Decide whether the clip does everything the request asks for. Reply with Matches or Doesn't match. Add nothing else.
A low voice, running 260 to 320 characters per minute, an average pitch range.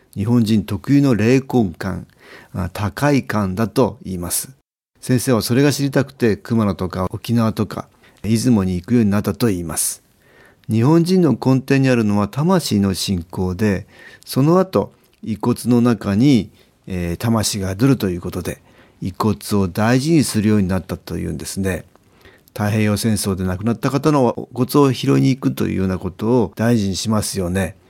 Matches